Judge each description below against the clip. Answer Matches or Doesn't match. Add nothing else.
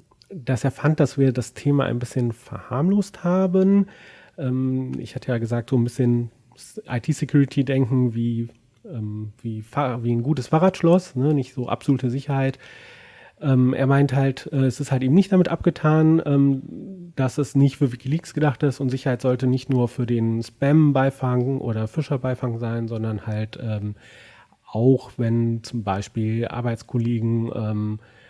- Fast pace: Doesn't match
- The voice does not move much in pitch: Doesn't match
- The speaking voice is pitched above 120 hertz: Matches